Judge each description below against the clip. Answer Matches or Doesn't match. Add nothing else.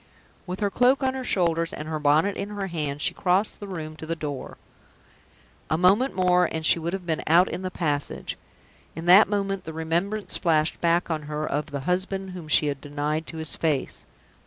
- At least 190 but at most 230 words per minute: Matches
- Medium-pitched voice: Matches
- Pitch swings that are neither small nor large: Matches